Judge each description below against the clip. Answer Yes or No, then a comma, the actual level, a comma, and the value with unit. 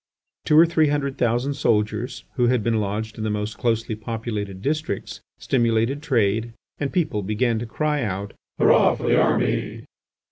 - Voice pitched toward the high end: No, low, 115 Hz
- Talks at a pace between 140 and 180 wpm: Yes, average, 165 wpm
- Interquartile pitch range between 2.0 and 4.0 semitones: No, average, 4.4 semitones